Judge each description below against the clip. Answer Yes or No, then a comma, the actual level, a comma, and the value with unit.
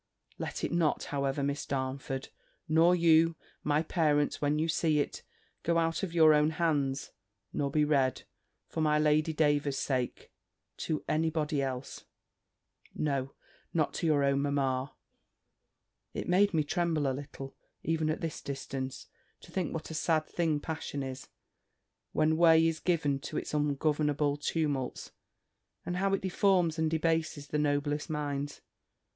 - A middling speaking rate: Yes, average, 150 wpm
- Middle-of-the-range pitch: Yes, medium, 150 Hz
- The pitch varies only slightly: Yes, narrow, 2.3 semitones